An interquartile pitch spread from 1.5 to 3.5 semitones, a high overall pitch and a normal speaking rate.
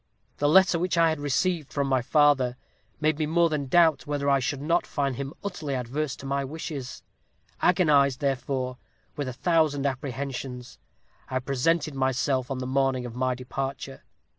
No: average, 2.9 semitones; medium, 140 Hz; average, 165 wpm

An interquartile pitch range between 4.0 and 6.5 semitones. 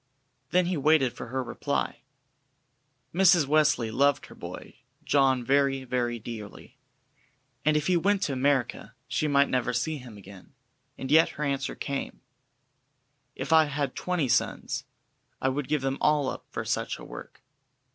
No: average, 3.1 semitones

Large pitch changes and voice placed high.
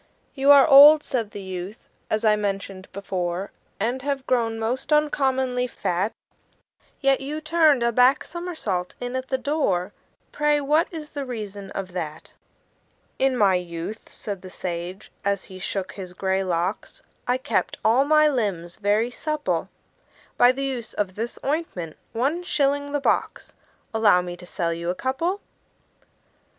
Yes: wide, 6.6 semitones; high, 230 Hz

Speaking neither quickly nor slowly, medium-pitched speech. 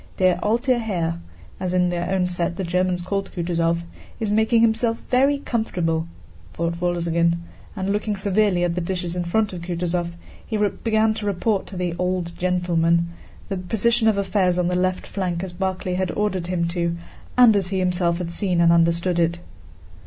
Yes: average, 180 wpm; medium, 180 Hz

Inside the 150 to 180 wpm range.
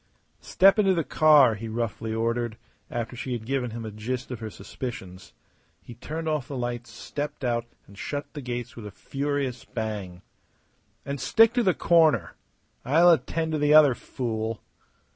Yes: average, 170 wpm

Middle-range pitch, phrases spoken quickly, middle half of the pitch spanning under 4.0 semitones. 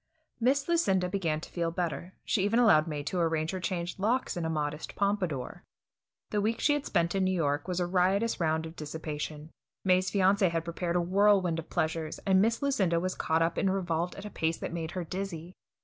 Yes: medium, 180 Hz; fast, 210 wpm; average, 3.3 semitones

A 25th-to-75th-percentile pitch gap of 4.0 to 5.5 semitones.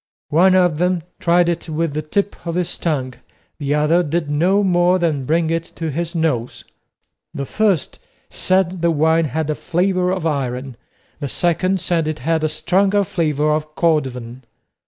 No: average, 2.9 semitones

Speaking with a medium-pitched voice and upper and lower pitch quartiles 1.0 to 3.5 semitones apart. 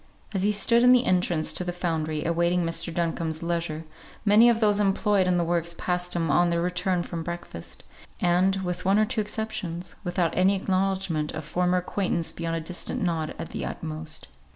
Yes: medium, 175 Hz; narrow, 2.5 semitones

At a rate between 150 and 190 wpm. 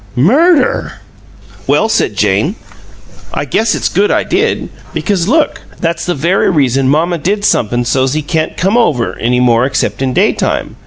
Yes: average, 155 wpm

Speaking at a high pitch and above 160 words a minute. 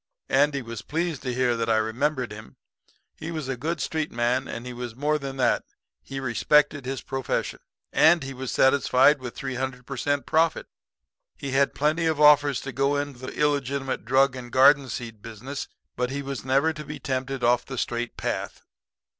No: low, 135 Hz; average, 190 wpm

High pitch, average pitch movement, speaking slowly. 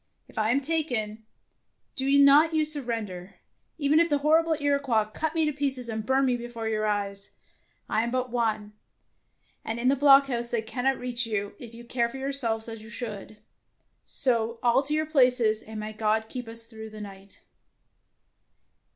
No: high, 240 Hz; average, 4.0 semitones; average, 180 wpm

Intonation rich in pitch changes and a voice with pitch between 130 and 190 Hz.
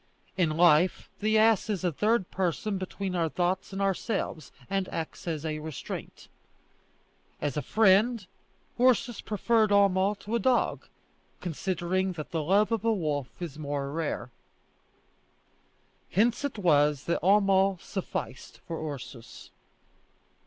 No: average, 4.7 semitones; medium, 185 Hz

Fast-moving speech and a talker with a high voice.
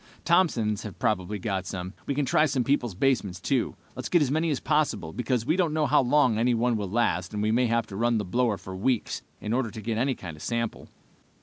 No: fast, 235 wpm; low, 115 Hz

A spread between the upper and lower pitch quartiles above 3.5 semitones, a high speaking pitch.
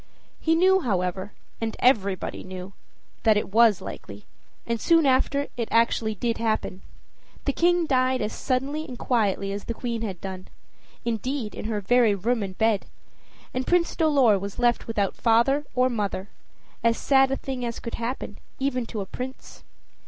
Yes: average, 4.2 semitones; high, 230 Hz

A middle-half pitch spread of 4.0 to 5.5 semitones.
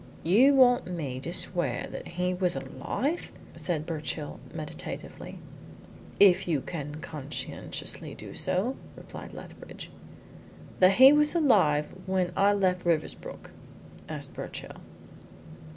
Yes: average, 5.1 semitones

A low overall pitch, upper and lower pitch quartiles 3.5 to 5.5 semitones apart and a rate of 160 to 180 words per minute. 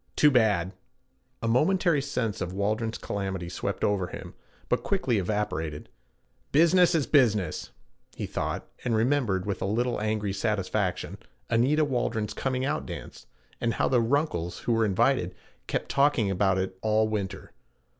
No: low, 110 Hz; average, 5.1 semitones; average, 145 wpm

